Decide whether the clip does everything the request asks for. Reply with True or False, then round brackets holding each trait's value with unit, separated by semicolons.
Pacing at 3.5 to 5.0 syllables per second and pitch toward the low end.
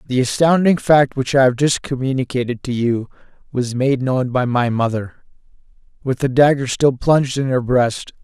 True (4.9 syllables/s; 130 Hz)